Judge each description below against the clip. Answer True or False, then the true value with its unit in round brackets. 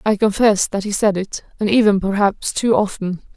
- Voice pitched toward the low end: False (200 Hz)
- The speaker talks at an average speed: True (195 wpm)